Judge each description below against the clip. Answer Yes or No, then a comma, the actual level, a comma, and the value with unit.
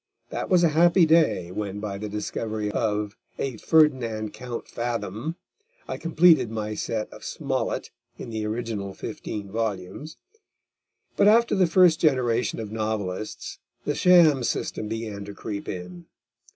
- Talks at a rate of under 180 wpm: Yes, average, 140 wpm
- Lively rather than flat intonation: Yes, wide, 6.6 semitones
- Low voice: Yes, low, 110 Hz